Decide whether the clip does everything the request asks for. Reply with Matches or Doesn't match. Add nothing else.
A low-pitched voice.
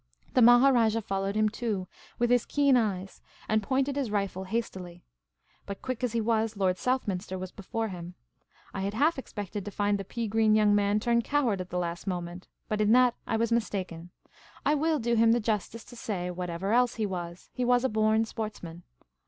Doesn't match